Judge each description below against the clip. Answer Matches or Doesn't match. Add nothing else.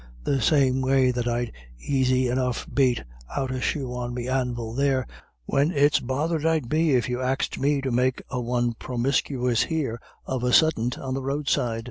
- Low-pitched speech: Matches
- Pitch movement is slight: Matches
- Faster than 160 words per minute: Matches